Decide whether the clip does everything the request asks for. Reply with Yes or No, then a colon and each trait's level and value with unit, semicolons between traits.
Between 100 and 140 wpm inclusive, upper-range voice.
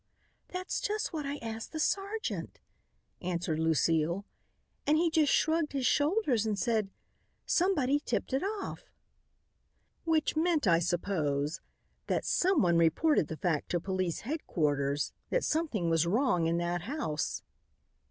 Yes: slow, 135 wpm; high, 225 Hz